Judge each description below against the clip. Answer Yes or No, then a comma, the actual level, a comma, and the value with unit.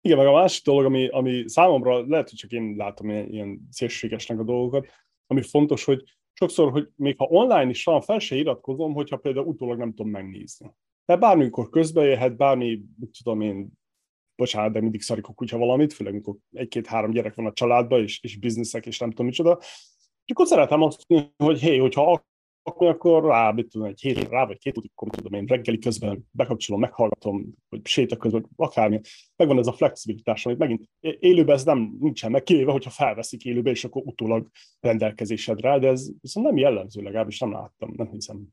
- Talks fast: Yes, fast, 200 wpm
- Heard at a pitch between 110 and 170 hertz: Yes, low, 120 Hz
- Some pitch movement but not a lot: Yes, average, 4.0 semitones